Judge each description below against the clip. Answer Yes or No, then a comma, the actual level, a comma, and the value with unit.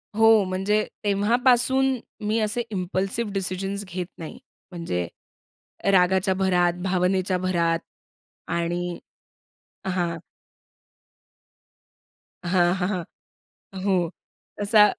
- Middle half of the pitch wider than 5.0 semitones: No, average, 2.8 semitones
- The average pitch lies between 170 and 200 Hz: Yes, high, 190 Hz